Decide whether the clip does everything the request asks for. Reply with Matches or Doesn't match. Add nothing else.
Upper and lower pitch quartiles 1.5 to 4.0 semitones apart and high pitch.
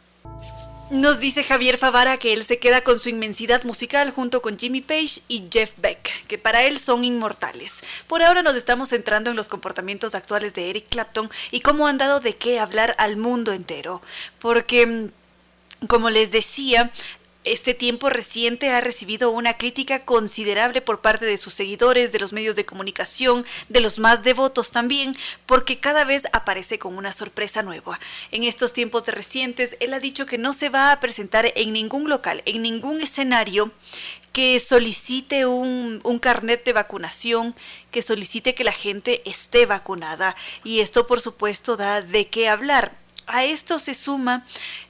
Matches